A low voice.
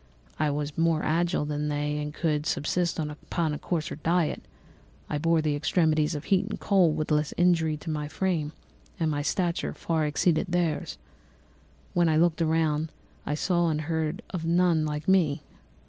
No: medium, 160 Hz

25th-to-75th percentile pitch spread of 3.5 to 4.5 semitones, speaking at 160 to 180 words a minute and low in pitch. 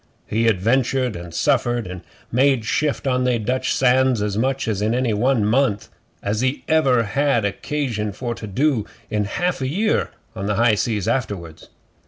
Yes: average, 4.0 semitones; average, 170 wpm; low, 120 Hz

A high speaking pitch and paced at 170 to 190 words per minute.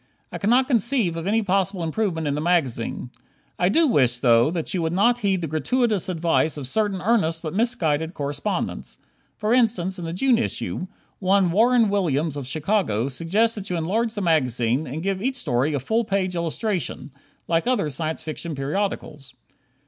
No: medium, 175 Hz; average, 175 wpm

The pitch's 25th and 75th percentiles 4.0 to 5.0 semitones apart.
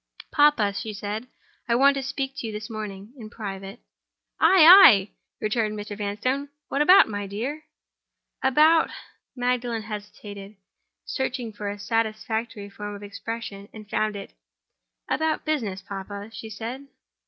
Yes: average, 4.3 semitones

